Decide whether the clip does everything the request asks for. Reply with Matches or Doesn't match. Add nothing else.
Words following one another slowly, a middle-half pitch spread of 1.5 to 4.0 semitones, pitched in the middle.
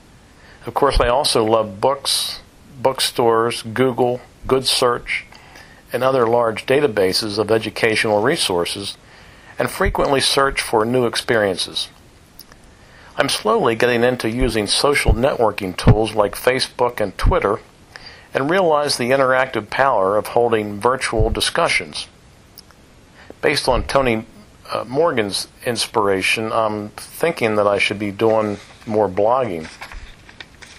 Doesn't match